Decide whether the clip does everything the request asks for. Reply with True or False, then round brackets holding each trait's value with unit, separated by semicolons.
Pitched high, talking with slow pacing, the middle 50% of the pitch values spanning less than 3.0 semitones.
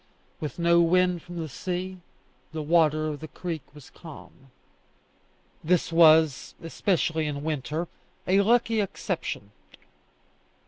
False (165 Hz; 120 wpm; 2.6 semitones)